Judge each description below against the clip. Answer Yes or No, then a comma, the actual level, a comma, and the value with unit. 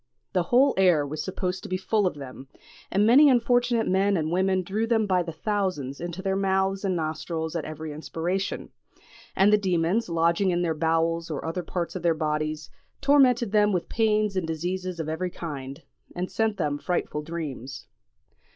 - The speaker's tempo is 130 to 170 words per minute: No, average, 180 wpm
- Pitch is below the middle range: No, medium, 180 Hz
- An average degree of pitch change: Yes, average, 3.7 semitones